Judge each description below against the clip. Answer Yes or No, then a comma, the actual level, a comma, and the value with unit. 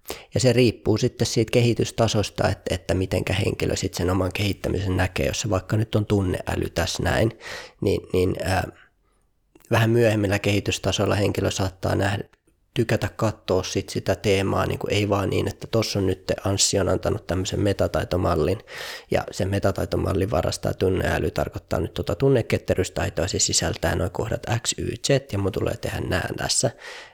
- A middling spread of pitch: Yes, average, 3.2 semitones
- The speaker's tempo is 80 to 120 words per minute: No, fast, 155 wpm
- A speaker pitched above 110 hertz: No, low, 100 Hz